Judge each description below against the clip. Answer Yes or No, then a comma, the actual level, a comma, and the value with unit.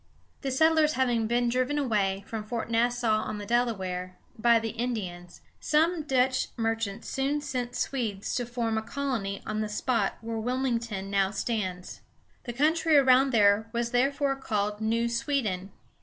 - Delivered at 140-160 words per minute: Yes, average, 155 wpm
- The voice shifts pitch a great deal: No, average, 3.6 semitones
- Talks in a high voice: Yes, high, 235 Hz